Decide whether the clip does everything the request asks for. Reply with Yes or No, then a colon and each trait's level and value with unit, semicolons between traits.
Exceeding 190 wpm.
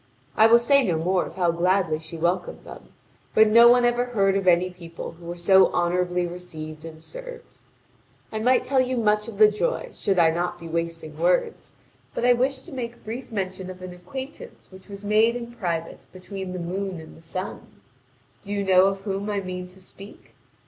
Yes: fast, 205 wpm